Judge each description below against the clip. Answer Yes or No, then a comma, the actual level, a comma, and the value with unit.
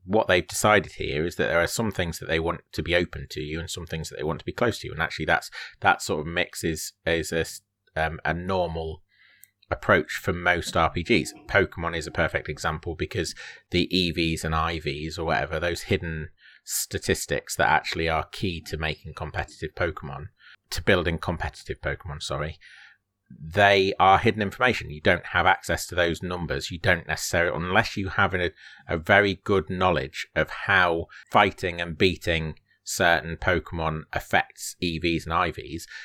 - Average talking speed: Yes, average, 180 wpm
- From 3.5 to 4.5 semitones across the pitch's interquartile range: No, average, 2.7 semitones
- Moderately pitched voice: No, very low, 85 Hz